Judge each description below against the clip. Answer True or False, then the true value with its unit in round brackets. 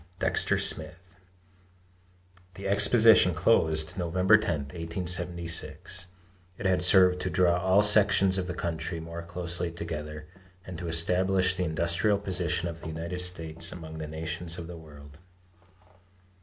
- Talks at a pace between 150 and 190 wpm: False (135 wpm)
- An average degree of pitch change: False (2.1 semitones)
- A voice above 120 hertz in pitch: False (85 Hz)